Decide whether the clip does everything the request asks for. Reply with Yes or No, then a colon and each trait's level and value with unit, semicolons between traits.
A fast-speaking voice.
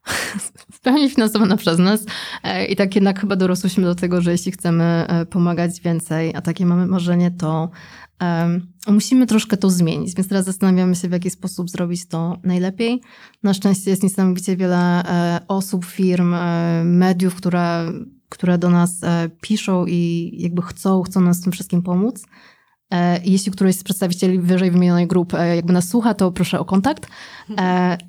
Yes: fast, 170 wpm